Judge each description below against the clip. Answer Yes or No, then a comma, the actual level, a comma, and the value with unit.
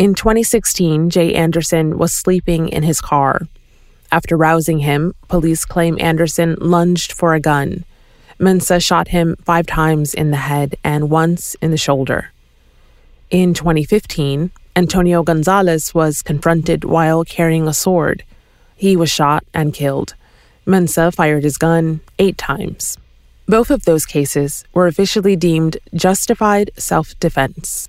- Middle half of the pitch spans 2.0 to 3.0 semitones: Yes, narrow, 2.4 semitones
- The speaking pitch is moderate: Yes, medium, 165 Hz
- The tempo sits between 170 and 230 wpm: No, slow, 135 wpm